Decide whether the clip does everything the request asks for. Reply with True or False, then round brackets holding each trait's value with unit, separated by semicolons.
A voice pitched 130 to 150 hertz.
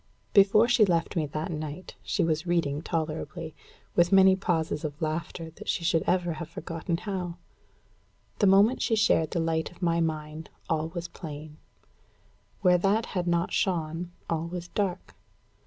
False (170 Hz)